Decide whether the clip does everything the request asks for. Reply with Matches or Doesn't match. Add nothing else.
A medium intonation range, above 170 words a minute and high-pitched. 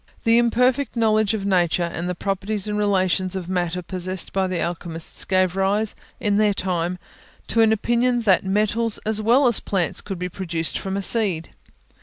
Matches